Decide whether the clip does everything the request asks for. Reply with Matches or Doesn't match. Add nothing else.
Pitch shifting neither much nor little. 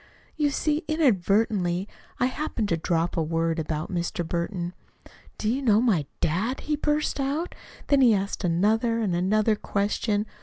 Doesn't match